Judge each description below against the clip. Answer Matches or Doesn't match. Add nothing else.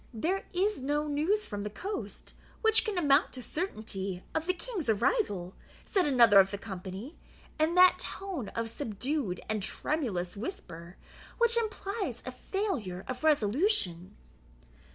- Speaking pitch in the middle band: Doesn't match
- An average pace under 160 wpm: Matches